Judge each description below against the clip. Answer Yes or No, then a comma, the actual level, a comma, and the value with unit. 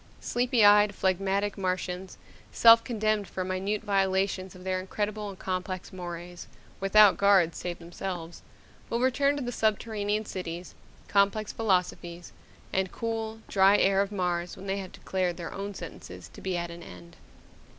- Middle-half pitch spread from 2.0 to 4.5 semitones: Yes, narrow, 2.4 semitones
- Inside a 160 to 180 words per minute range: No, average, 150 wpm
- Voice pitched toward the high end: Yes, high, 195 Hz